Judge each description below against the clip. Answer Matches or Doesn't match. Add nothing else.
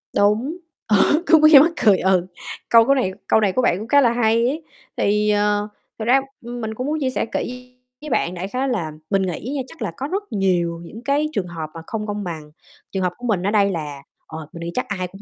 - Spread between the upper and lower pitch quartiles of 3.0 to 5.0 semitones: Doesn't match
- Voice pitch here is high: Matches